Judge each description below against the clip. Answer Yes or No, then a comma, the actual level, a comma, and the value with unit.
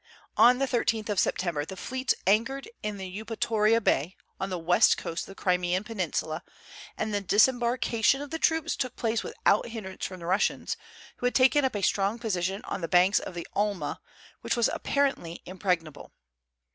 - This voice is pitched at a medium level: No, high, 205 Hz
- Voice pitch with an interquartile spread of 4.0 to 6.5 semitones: Yes, average, 4.5 semitones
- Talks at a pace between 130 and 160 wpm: No, average, 175 wpm